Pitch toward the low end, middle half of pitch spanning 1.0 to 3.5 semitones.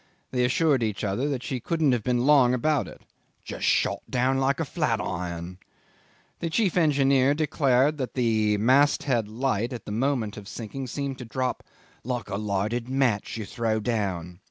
No: low, 125 Hz; average, 4.3 semitones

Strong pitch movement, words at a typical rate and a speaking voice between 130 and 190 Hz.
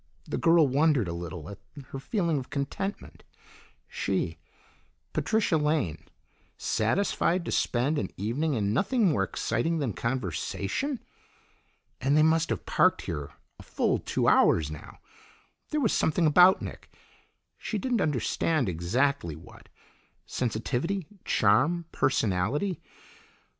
No: wide, 7.8 semitones; slow, 120 wpm; medium, 140 Hz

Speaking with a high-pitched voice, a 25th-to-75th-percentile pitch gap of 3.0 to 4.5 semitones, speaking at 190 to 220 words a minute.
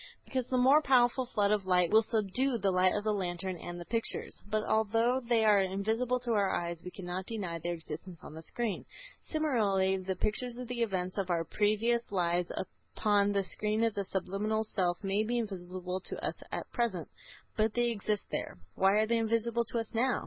Yes: high, 210 Hz; average, 3.8 semitones; average, 200 wpm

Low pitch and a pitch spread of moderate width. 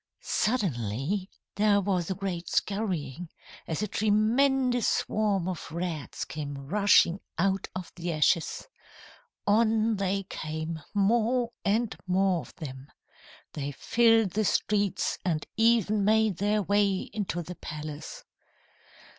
No: high, 195 Hz; average, 4.2 semitones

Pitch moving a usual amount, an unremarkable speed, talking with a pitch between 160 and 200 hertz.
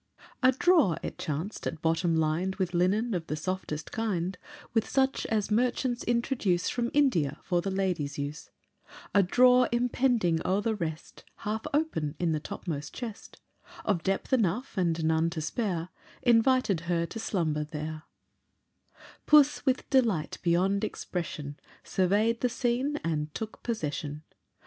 No: wide, 6.6 semitones; average, 145 wpm; high, 190 Hz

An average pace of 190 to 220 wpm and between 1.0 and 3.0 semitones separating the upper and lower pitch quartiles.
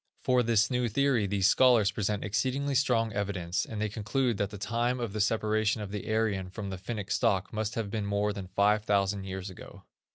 Yes: fast, 205 wpm; narrow, 2.4 semitones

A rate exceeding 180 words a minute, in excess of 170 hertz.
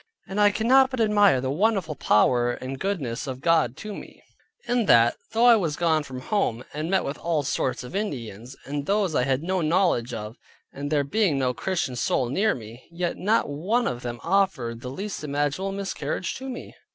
No: average, 200 wpm; medium, 155 Hz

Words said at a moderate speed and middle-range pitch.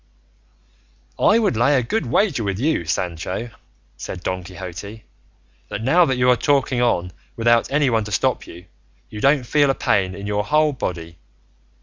No: average, 165 wpm; low, 115 Hz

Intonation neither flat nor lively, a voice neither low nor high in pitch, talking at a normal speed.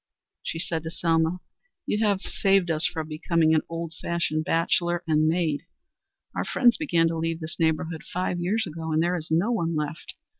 No: narrow, 1.7 semitones; medium, 165 Hz; average, 185 wpm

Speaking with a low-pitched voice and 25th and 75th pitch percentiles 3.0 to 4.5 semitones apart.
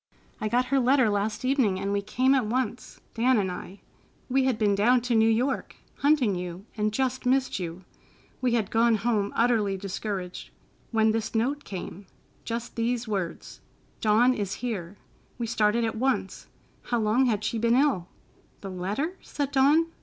No: high, 225 Hz; average, 3.8 semitones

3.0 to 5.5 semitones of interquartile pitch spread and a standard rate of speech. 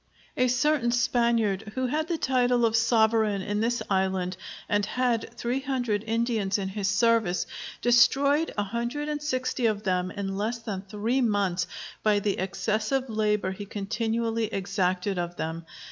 Yes: average, 3.5 semitones; average, 155 wpm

